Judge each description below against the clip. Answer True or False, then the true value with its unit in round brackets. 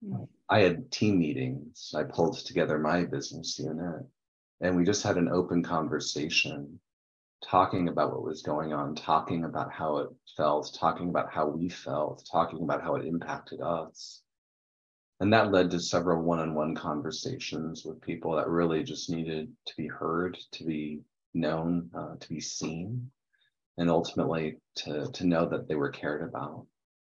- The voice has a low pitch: True (85 Hz)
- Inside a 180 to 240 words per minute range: False (165 wpm)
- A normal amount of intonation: False (2.1 semitones)